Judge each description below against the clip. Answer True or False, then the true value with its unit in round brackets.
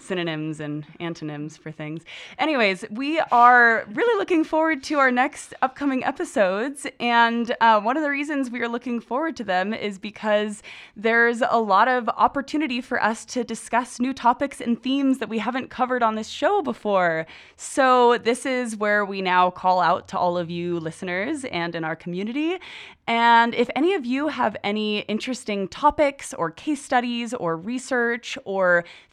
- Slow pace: False (170 wpm)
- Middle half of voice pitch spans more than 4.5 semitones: True (5.1 semitones)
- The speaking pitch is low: False (235 Hz)